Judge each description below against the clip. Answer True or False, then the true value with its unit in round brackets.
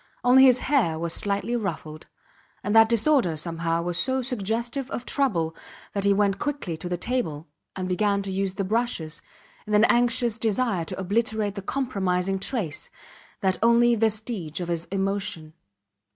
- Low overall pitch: False (200 Hz)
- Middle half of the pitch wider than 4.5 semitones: True (5.1 semitones)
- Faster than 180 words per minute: False (160 wpm)